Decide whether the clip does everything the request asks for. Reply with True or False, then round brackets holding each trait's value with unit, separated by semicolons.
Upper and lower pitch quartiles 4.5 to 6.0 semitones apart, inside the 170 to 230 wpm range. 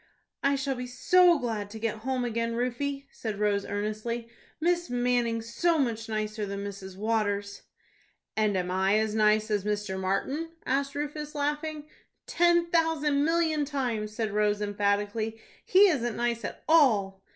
False (5.4 semitones; 150 wpm)